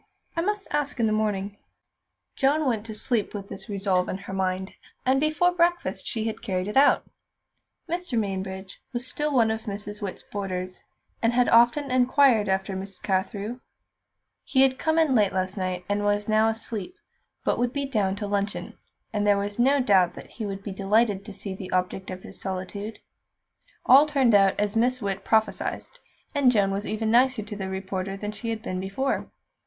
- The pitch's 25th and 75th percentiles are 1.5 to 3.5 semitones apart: No, average, 4.3 semitones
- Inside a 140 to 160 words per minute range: No, average, 190 wpm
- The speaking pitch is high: Yes, high, 210 Hz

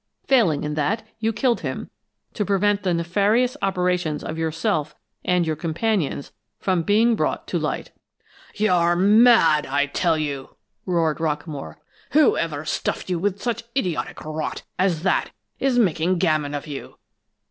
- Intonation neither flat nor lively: Yes, average, 4.9 semitones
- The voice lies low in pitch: No, medium, 175 Hz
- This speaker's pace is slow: No, average, 145 wpm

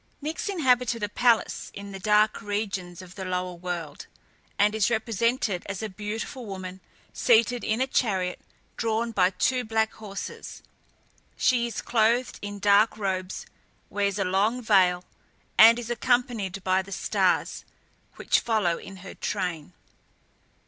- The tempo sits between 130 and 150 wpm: Yes, average, 140 wpm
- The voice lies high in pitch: Yes, high, 210 Hz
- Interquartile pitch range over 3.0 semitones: Yes, average, 3.6 semitones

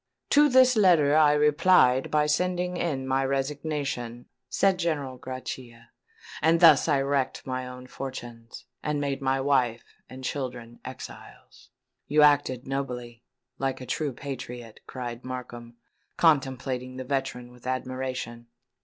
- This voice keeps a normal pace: No, slow, 125 wpm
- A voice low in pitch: Yes, low, 130 Hz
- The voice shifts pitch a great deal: No, average, 2.9 semitones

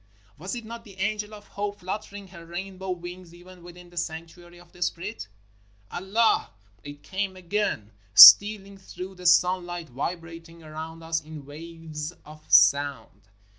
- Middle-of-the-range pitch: Yes, medium, 175 Hz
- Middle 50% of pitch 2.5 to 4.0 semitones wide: Yes, average, 3.1 semitones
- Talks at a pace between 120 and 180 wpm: Yes, average, 155 wpm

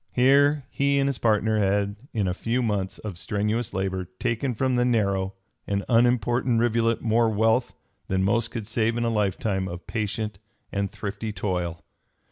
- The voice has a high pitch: No, low, 110 Hz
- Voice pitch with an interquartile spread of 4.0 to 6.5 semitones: No, average, 3.2 semitones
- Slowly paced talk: No, average, 165 wpm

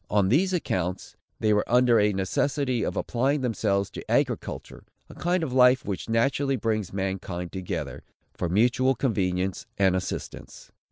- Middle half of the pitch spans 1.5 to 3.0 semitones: No, average, 5.3 semitones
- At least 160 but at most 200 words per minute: No, average, 150 wpm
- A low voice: Yes, low, 110 Hz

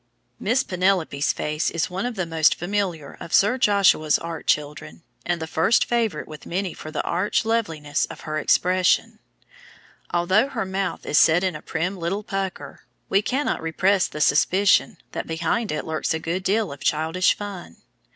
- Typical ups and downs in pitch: Yes, average, 3.9 semitones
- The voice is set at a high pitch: No, medium, 180 Hz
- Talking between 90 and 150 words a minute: No, average, 175 wpm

